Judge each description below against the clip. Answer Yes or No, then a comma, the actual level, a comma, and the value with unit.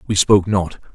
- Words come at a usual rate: Yes, average, 190 wpm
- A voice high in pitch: No, very low, 95 Hz